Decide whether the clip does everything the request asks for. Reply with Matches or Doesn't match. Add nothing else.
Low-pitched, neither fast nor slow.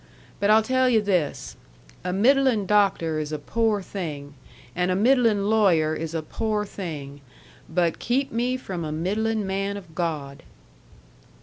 Doesn't match